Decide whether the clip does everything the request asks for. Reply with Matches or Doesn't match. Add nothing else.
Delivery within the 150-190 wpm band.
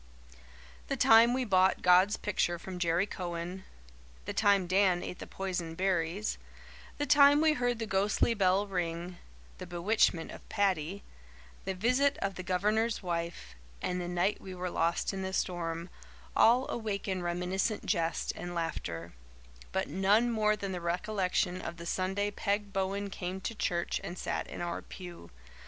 Matches